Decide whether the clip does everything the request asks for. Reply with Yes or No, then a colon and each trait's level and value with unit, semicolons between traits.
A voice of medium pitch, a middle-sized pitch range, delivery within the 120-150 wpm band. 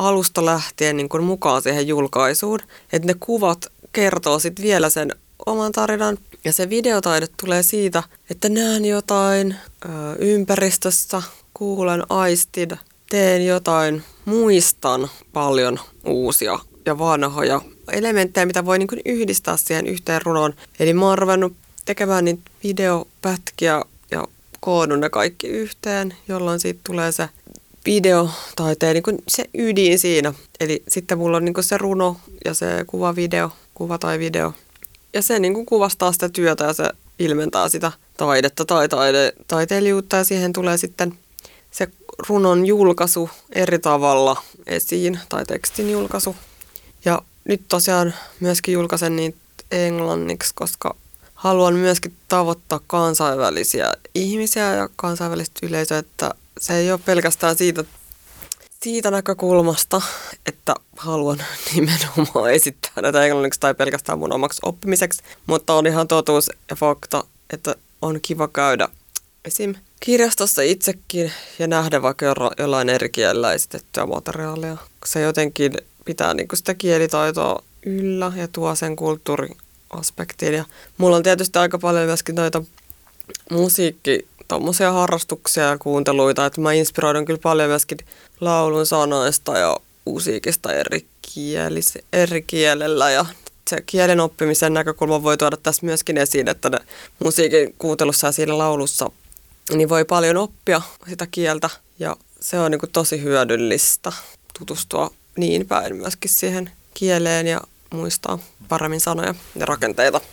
Yes: medium, 170 Hz; average, 3.2 semitones; average, 130 wpm